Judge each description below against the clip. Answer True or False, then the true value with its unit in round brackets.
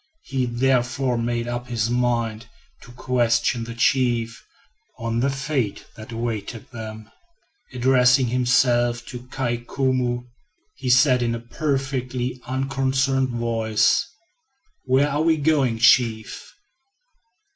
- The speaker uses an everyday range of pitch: False (2.0 semitones)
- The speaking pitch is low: True (125 Hz)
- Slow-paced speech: True (115 wpm)